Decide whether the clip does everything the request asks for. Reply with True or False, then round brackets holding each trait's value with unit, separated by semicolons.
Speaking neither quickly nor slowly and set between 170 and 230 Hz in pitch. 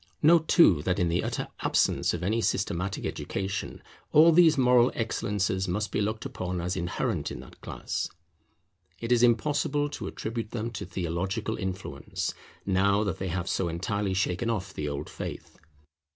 False (165 wpm; 100 Hz)